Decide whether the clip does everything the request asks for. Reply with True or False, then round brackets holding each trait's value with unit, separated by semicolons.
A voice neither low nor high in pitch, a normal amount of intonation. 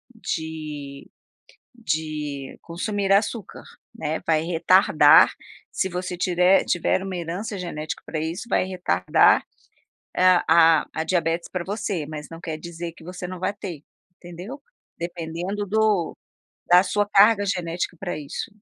True (175 Hz; 3.2 semitones)